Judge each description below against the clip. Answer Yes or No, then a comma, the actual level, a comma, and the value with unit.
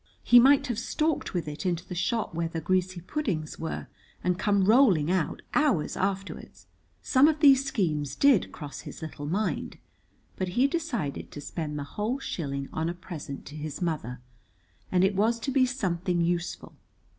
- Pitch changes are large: Yes, wide, 7.0 semitones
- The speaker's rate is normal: Yes, average, 175 wpm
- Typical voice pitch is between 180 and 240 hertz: Yes, medium, 185 Hz